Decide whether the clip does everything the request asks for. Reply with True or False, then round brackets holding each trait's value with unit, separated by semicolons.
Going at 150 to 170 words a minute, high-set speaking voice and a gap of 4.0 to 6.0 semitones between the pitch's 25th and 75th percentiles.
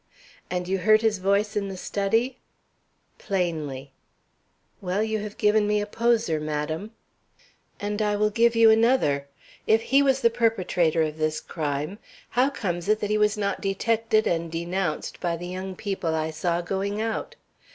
True (165 wpm; 200 Hz; 4.3 semitones)